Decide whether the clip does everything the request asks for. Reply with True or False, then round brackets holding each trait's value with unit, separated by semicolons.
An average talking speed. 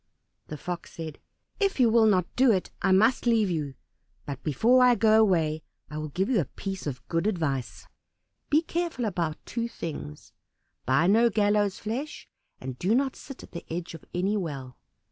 True (185 wpm)